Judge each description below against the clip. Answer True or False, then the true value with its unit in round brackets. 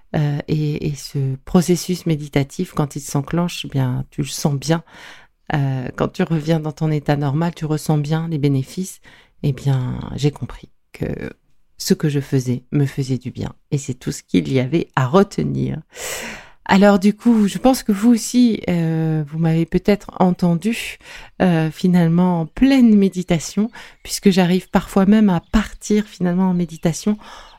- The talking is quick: False (165 wpm)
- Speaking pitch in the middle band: True (165 Hz)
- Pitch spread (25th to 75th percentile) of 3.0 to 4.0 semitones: False (4.8 semitones)